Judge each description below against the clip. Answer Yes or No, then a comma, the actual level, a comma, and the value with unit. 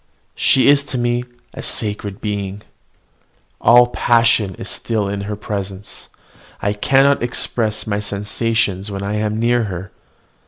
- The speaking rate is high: No, average, 140 wpm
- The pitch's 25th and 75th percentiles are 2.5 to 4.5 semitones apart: Yes, average, 2.9 semitones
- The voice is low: Yes, low, 105 Hz